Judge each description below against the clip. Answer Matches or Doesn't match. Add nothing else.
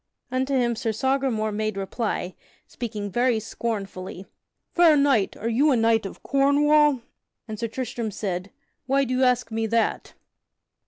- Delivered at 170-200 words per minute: Doesn't match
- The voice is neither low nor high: Doesn't match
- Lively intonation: Doesn't match